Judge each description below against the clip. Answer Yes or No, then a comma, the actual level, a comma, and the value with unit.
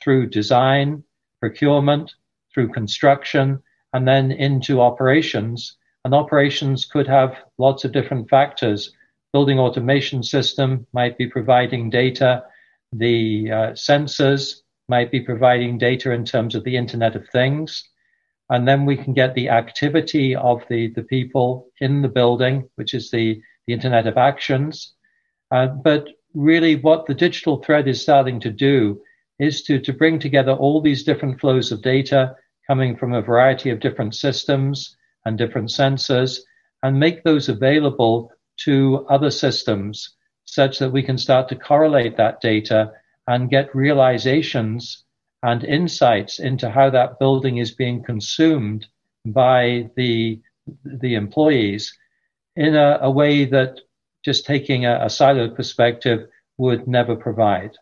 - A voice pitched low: Yes, low, 130 Hz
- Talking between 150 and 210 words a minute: No, average, 140 wpm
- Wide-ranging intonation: No, narrow, 2.5 semitones